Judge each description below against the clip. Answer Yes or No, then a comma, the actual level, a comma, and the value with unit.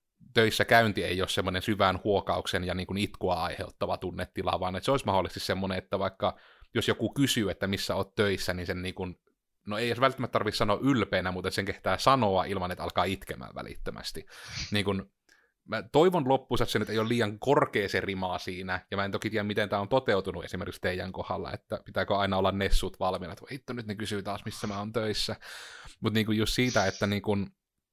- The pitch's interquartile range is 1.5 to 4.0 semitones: Yes, average, 2.7 semitones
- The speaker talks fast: Yes, fast, 210 wpm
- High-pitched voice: No, low, 100 Hz